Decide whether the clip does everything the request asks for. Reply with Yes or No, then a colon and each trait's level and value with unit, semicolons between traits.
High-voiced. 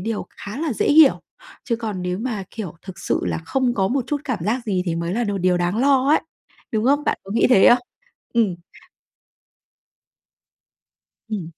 Yes: high, 220 Hz